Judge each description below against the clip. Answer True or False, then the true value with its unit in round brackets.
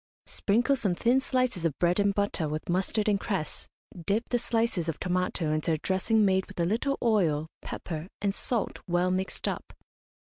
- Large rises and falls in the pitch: False (4.4 semitones)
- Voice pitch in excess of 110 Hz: True (190 Hz)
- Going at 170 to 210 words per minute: True (180 wpm)